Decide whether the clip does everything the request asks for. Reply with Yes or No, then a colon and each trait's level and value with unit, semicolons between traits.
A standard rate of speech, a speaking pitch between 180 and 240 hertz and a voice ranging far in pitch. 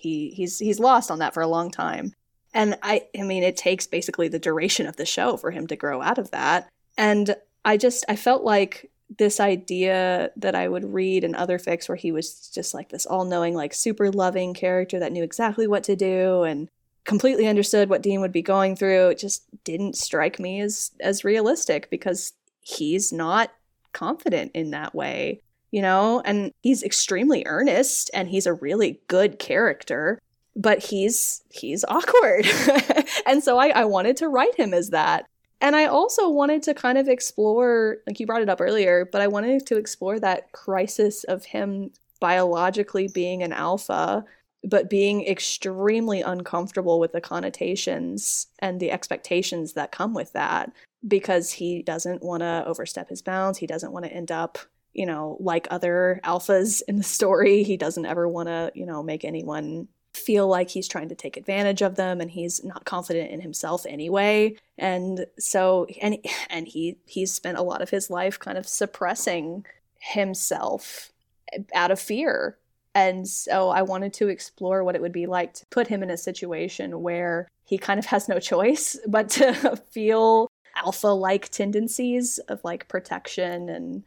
No: average, 180 wpm; high, 190 Hz; average, 3.2 semitones